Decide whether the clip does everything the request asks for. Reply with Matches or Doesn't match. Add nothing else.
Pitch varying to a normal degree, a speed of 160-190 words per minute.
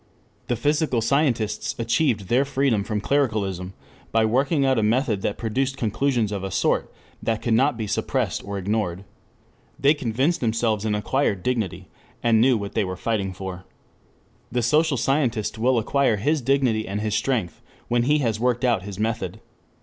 Matches